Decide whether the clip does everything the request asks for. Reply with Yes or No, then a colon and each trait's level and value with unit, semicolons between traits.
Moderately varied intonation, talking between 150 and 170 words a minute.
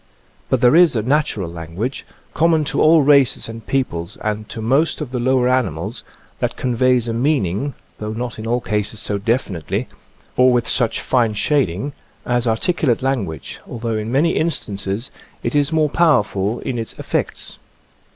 Yes: average, 4.3 semitones; average, 160 wpm